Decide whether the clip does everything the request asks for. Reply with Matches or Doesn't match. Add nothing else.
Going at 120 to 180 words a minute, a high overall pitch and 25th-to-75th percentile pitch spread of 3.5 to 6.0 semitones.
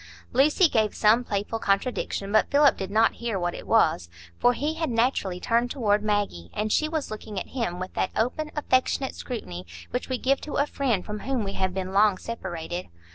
Doesn't match